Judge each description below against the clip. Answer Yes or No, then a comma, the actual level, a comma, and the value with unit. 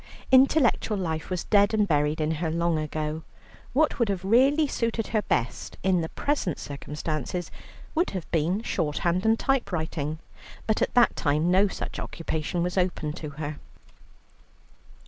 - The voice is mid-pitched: Yes, medium, 175 Hz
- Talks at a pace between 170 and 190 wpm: No, average, 155 wpm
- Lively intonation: Yes, wide, 5.8 semitones